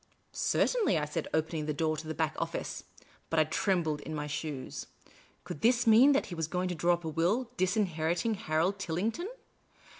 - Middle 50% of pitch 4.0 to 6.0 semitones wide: Yes, average, 4.4 semitones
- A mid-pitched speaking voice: Yes, medium, 170 Hz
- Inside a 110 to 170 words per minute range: No, average, 190 wpm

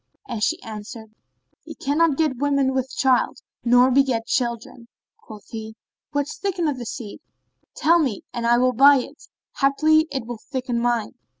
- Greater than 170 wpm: No, average, 160 wpm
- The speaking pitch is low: No, very high, 255 Hz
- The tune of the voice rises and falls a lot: No, average, 3.2 semitones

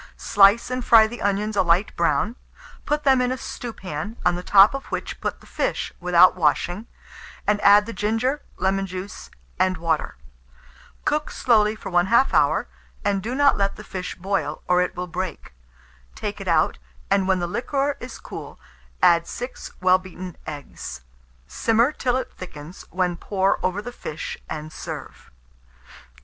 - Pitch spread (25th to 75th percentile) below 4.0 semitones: No, average, 4.5 semitones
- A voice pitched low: No, high, 195 Hz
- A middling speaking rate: Yes, average, 165 wpm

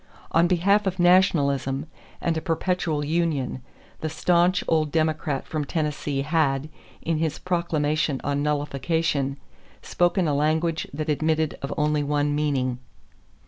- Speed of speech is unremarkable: No, slow, 130 wpm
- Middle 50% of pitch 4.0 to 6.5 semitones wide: No, narrow, 2.6 semitones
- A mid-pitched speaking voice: Yes, medium, 155 Hz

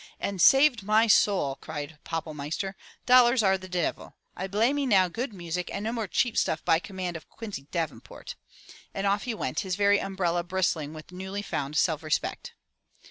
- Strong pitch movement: No, average, 4.4 semitones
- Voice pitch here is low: No, high, 190 Hz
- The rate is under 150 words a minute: No, average, 180 wpm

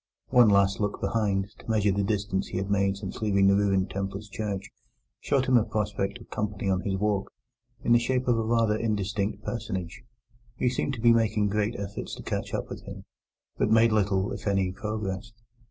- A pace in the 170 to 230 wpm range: Yes, average, 200 wpm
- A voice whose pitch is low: Yes, low, 105 Hz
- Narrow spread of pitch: Yes, narrow, 2.2 semitones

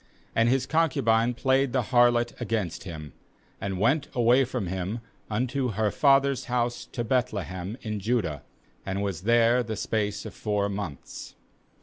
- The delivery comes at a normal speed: Yes, average, 150 wpm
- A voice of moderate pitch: No, low, 115 Hz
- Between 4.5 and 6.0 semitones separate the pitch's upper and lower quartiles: No, average, 3.7 semitones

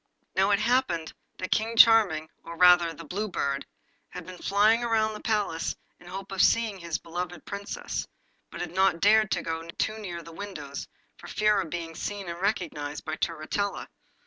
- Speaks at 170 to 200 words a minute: Yes, average, 185 wpm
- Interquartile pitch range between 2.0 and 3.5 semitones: No, average, 4.0 semitones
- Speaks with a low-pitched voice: No, medium, 185 Hz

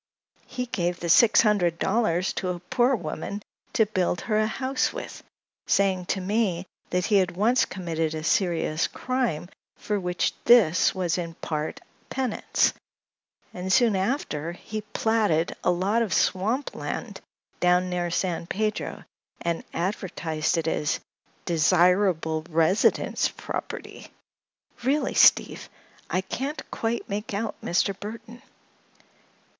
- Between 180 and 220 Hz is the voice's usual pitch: Yes, medium, 185 Hz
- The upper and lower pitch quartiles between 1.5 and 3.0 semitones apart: No, average, 4.1 semitones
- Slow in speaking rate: Yes, slow, 130 wpm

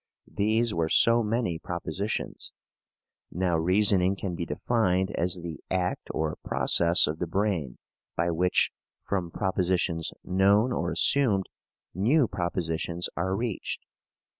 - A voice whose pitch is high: No, very low, 90 Hz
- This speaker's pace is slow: Yes, slow, 120 wpm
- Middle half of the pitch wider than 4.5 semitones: No, average, 3.3 semitones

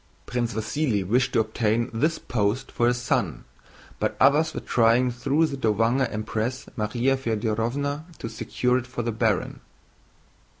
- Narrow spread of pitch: No, average, 3.1 semitones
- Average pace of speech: Yes, average, 145 wpm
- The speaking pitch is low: Yes, low, 120 Hz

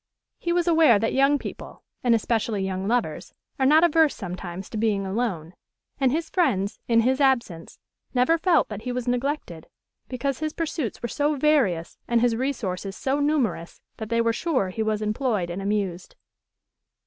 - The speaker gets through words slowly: No, average, 170 wpm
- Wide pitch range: Yes, wide, 6.0 semitones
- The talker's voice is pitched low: No, high, 235 Hz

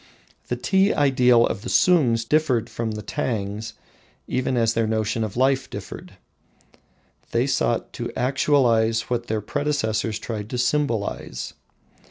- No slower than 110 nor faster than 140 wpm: Yes, slow, 135 wpm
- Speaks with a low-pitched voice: Yes, low, 115 Hz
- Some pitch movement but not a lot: Yes, average, 3.0 semitones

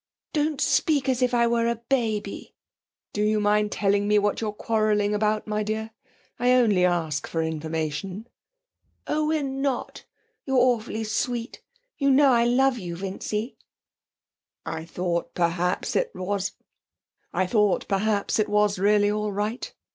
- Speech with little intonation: No, average, 3.4 semitones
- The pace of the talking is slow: Yes, slow, 130 wpm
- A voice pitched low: No, high, 210 Hz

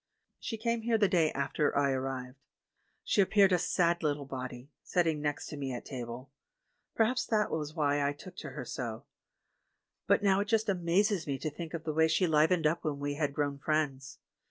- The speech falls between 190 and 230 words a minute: Yes, average, 200 wpm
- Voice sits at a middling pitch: Yes, medium, 155 Hz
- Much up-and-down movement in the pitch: No, average, 4.5 semitones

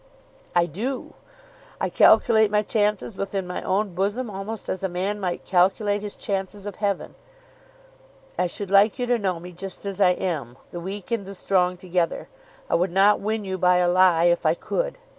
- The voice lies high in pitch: Yes, high, 195 Hz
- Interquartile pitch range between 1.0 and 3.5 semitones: Yes, narrow, 2.4 semitones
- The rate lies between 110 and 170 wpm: No, average, 190 wpm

